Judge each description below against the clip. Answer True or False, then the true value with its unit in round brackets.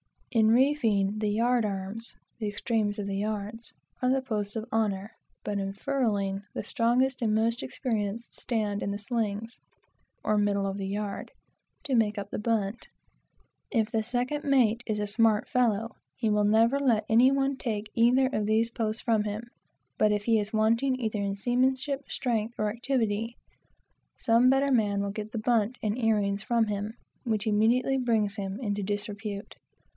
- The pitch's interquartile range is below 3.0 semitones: True (2.6 semitones)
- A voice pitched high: True (220 Hz)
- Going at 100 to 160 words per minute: False (170 wpm)